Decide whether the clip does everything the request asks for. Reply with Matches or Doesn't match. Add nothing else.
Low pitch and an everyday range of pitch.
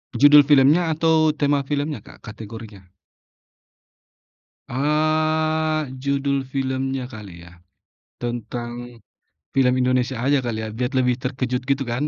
Matches